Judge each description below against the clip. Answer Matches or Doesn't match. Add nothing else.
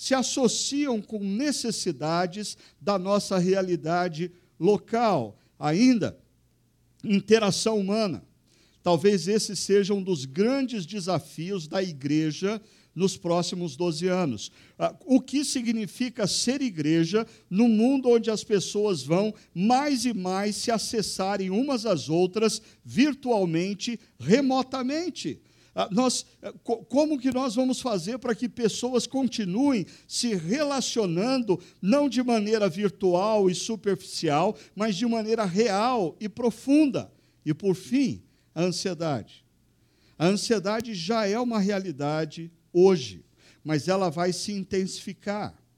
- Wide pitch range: Doesn't match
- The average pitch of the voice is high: Matches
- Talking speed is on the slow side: Matches